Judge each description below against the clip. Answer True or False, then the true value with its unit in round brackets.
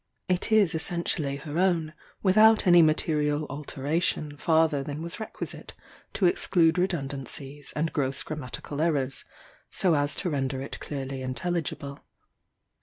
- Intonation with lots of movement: False (3.6 semitones)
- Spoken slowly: True (125 wpm)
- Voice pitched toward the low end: False (155 Hz)